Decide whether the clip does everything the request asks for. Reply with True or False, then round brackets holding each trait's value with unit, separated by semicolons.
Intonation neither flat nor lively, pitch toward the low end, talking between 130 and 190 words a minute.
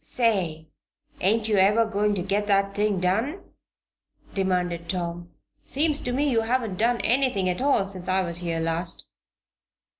False (4.1 semitones; 200 Hz; 155 wpm)